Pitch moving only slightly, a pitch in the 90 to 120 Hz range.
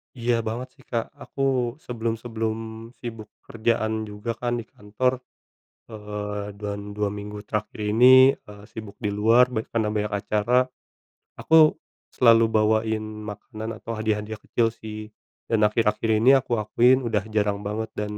Yes: narrow, 1.8 semitones; low, 110 Hz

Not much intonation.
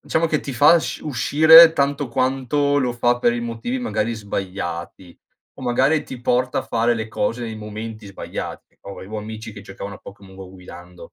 No: average, 5.1 semitones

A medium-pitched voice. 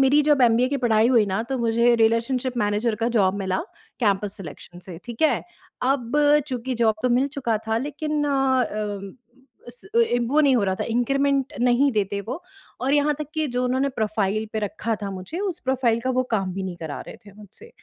No: high, 235 Hz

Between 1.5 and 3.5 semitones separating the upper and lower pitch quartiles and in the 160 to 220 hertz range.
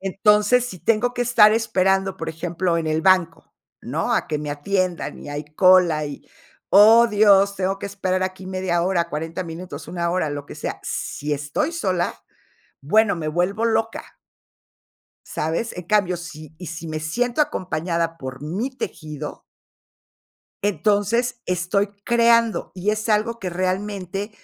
No: average, 4.1 semitones; medium, 185 Hz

